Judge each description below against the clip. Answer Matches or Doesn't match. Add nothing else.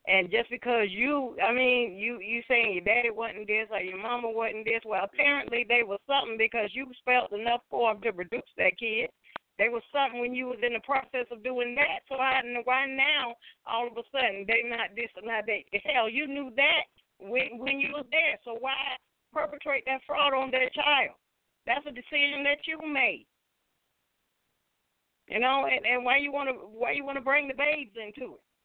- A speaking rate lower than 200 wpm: Doesn't match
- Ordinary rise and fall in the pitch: Matches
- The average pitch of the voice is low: Doesn't match